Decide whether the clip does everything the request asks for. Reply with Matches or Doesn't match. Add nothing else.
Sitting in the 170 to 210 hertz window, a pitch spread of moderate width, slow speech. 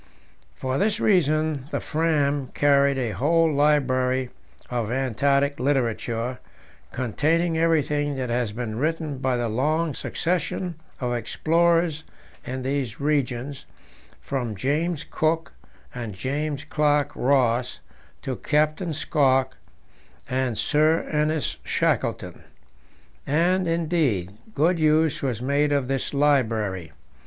Doesn't match